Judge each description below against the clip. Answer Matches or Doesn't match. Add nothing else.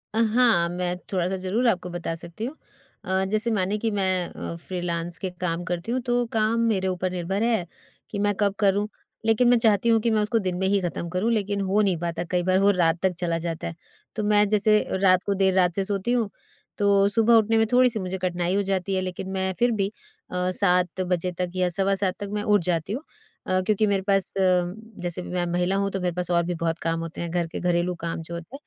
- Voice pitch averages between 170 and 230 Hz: Matches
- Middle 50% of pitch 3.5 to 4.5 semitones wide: Doesn't match